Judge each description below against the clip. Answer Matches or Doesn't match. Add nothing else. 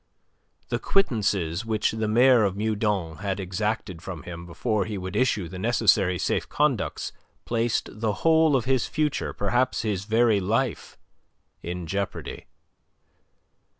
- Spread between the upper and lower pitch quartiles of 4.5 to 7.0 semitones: Doesn't match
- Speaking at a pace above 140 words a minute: Doesn't match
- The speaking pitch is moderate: Doesn't match